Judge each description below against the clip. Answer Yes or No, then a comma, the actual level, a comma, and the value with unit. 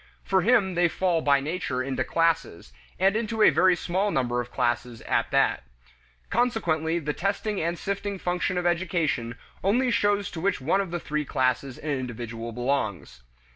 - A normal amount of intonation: No, wide, 6.8 semitones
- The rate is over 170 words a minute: No, average, 165 wpm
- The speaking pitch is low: No, medium, 165 Hz